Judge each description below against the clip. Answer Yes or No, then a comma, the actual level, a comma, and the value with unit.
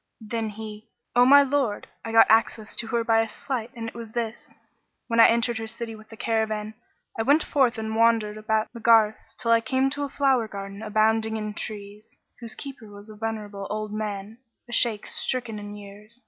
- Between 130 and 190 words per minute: No, fast, 205 wpm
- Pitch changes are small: Yes, narrow, 1.6 semitones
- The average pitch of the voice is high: Yes, high, 225 Hz